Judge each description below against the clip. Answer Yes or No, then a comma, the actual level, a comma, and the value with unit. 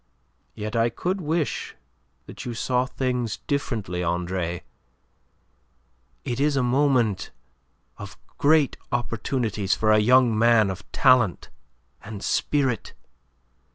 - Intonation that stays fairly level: No, average, 3.8 semitones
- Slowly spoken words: Yes, slow, 110 wpm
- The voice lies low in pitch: Yes, low, 120 Hz